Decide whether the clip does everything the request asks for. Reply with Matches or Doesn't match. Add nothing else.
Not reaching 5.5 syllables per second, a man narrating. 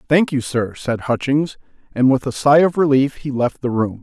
Matches